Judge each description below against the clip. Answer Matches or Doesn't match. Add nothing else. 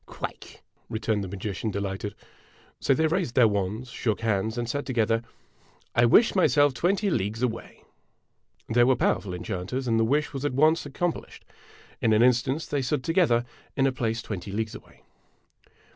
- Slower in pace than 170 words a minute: Doesn't match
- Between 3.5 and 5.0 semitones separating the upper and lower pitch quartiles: Matches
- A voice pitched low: Matches